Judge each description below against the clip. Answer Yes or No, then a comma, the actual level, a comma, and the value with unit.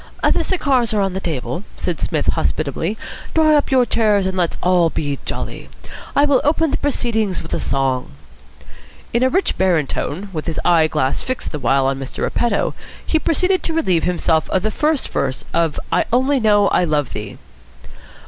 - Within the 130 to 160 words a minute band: No, average, 180 wpm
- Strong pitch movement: Yes, wide, 8.7 semitones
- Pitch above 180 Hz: Yes, high, 190 Hz